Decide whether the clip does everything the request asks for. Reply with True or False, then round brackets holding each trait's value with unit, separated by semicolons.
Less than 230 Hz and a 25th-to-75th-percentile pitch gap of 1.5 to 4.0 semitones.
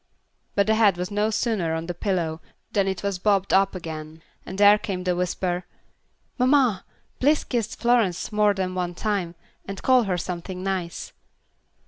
True (190 Hz; 2.9 semitones)